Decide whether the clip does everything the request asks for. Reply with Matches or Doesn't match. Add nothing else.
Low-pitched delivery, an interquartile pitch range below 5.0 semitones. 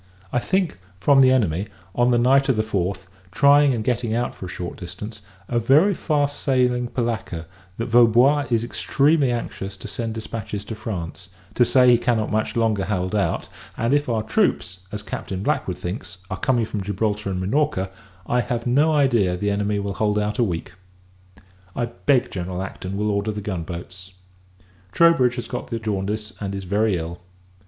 Matches